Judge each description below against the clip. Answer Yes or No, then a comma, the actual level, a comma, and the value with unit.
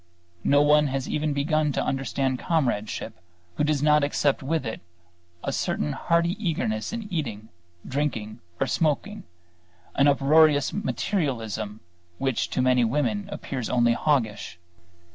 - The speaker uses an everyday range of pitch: Yes, average, 4.1 semitones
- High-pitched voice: No, medium, 140 Hz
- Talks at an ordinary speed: No, slow, 130 wpm